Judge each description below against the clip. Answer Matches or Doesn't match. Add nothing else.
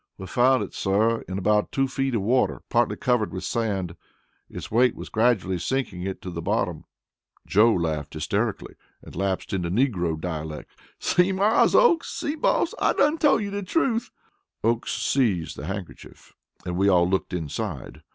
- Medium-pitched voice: Doesn't match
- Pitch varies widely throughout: Matches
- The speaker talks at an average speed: Matches